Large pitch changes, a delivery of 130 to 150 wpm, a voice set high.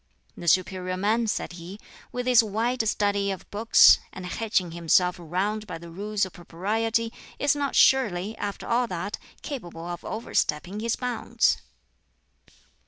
No: average, 4.1 semitones; average, 145 wpm; high, 205 Hz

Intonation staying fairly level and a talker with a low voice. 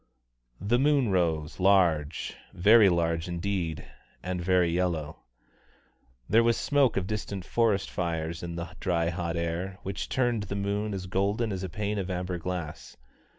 No: average, 3.3 semitones; very low, 90 Hz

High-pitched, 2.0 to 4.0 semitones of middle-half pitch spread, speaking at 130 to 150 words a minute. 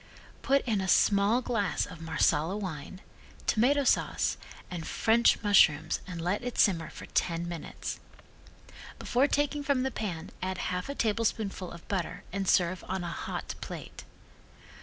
No: high, 195 Hz; average, 5.1 semitones; average, 145 wpm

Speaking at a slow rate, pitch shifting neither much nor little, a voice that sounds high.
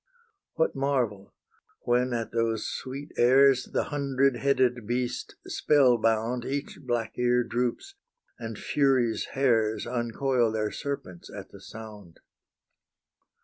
No: slow, 115 wpm; average, 3.1 semitones; low, 120 Hz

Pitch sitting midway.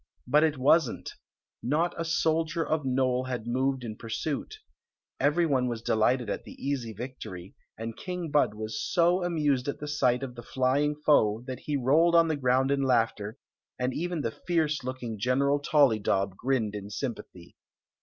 No: low, 130 Hz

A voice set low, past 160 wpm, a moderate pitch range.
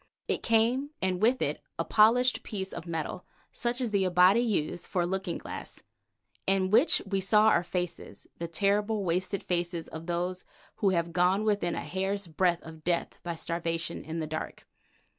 No: medium, 185 Hz; average, 180 wpm; average, 3.5 semitones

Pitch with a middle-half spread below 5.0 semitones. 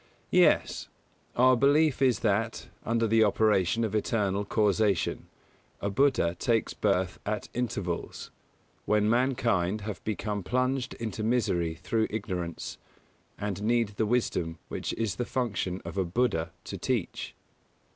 Yes: average, 3.4 semitones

